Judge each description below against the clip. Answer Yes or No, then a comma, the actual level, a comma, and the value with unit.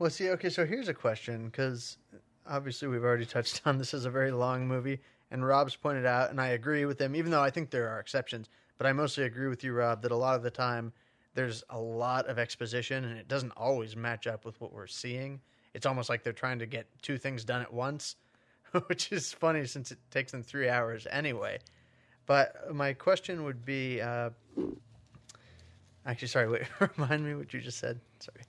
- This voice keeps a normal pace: No, fast, 215 wpm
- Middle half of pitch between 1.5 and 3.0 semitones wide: Yes, narrow, 2.6 semitones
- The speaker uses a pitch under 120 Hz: No, low, 130 Hz